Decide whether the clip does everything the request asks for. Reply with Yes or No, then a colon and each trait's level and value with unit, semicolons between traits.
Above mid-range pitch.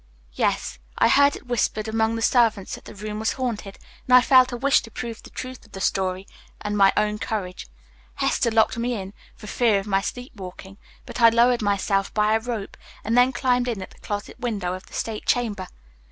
Yes: high, 220 Hz